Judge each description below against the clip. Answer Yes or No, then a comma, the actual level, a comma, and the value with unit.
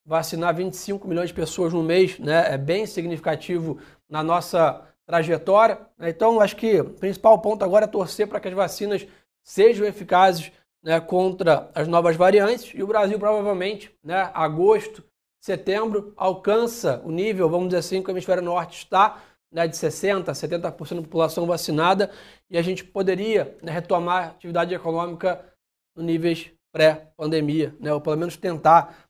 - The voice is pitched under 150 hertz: No, medium, 180 Hz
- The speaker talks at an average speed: Yes, average, 155 wpm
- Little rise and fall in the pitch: No, average, 3.2 semitones